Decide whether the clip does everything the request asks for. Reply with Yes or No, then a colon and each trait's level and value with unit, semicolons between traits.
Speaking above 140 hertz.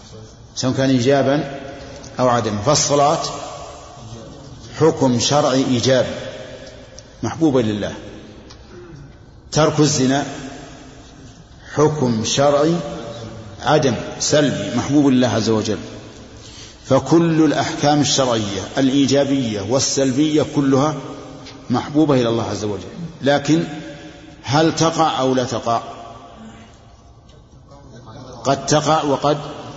No: low, 135 Hz